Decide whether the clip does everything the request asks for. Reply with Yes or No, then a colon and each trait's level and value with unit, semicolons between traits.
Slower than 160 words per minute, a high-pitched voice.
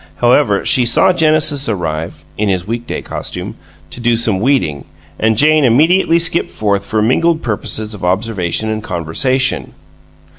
No: average, 145 wpm; low, 115 Hz